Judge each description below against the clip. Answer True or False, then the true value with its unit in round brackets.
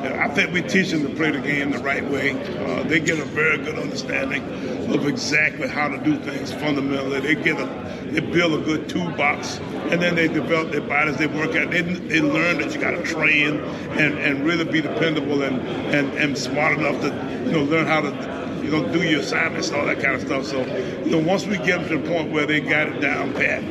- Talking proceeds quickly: True (235 wpm)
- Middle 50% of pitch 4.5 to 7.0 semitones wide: False (3.3 semitones)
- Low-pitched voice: False (150 Hz)